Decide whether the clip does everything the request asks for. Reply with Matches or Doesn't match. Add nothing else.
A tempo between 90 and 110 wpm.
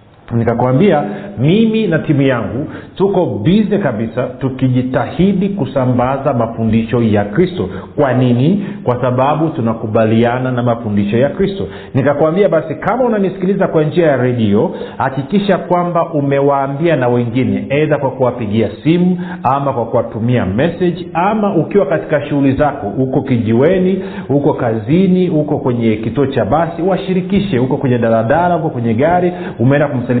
Doesn't match